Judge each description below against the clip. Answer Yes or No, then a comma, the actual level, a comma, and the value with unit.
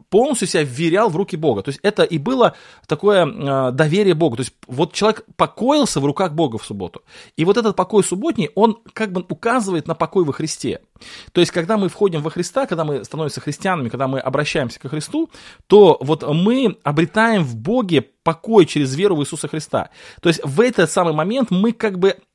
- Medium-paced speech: No, fast, 200 wpm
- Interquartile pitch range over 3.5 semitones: Yes, wide, 5.5 semitones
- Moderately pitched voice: Yes, medium, 170 Hz